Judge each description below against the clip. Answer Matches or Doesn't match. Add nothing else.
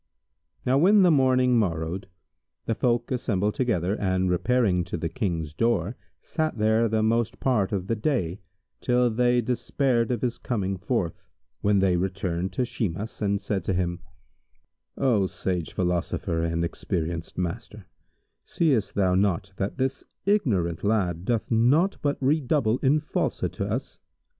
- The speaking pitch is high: Doesn't match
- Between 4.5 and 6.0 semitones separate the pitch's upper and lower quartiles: Matches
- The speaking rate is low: Doesn't match